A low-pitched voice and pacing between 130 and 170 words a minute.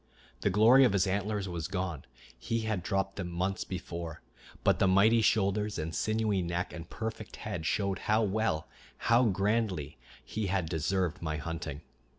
Yes: very low, 95 Hz; average, 165 wpm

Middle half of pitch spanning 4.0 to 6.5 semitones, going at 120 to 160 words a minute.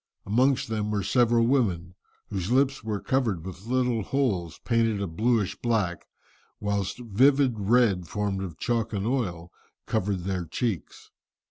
Yes: average, 4.3 semitones; average, 140 wpm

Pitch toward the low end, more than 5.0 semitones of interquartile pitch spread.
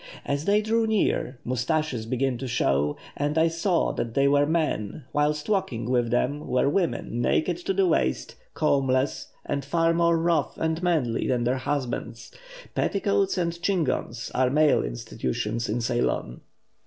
No: medium, 145 Hz; wide, 5.6 semitones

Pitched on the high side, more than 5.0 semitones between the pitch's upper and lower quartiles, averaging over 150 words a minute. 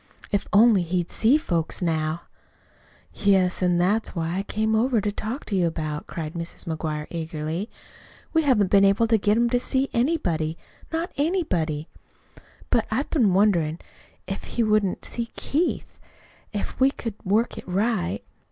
Yes: high, 200 Hz; wide, 5.5 semitones; average, 160 wpm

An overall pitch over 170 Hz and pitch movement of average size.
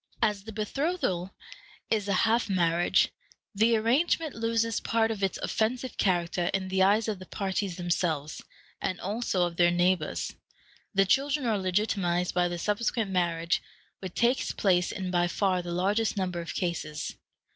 Yes: high, 190 Hz; average, 4.0 semitones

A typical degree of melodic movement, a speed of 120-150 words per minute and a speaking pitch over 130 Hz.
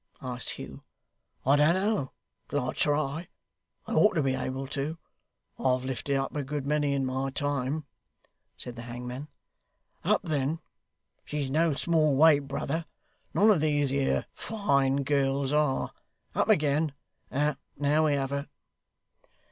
No: narrow, 2.1 semitones; average, 140 wpm; medium, 140 Hz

